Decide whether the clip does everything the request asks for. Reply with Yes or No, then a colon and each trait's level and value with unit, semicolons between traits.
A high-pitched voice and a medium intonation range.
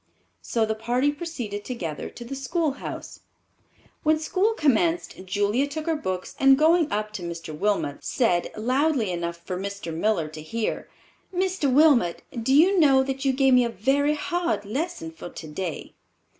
No: very high, 255 Hz; wide, 7.3 semitones